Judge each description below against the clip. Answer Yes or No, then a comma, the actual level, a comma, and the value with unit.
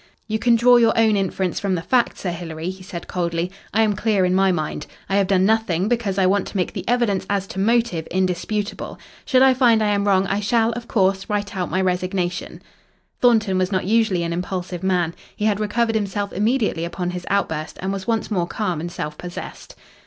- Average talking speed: No, fast, 215 wpm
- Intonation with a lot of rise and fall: No, average, 3.4 semitones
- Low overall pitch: No, high, 195 Hz